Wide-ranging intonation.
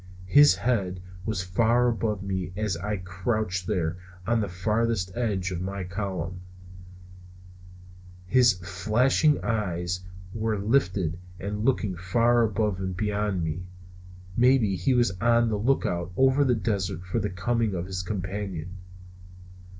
No: average, 4.1 semitones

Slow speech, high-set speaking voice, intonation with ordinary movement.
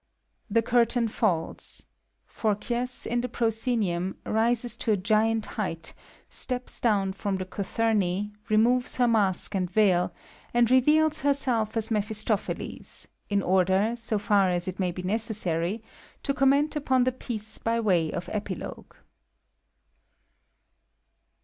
Yes: slow, 130 wpm; high, 220 Hz; average, 3.7 semitones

